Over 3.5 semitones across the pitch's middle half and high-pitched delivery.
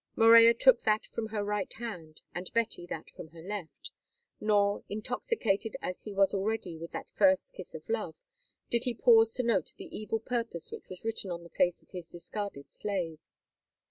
Yes: average, 4.2 semitones; high, 210 Hz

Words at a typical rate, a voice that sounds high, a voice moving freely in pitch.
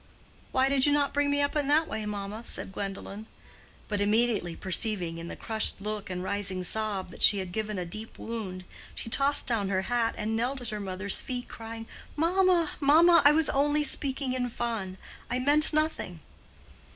Yes: average, 190 wpm; high, 225 Hz; wide, 6.0 semitones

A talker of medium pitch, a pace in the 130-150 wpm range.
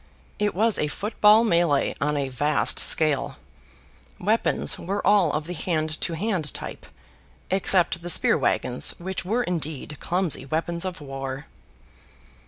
Yes: medium, 170 Hz; average, 145 wpm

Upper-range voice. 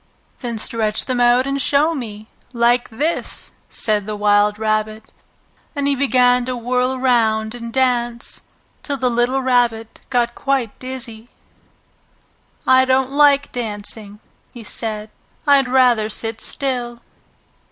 Yes: high, 240 Hz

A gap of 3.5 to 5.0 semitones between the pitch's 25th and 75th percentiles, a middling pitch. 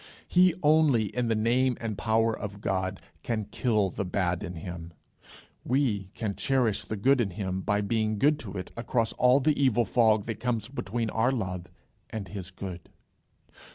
No: average, 3.9 semitones; low, 110 Hz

